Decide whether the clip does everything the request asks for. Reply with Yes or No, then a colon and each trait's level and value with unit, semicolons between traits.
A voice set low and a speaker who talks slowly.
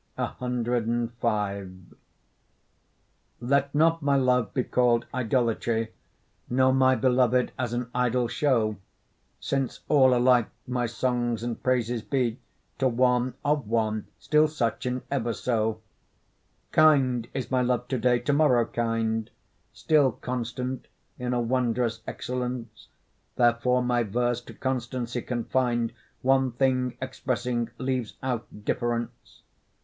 Yes: low, 125 Hz; slow, 120 wpm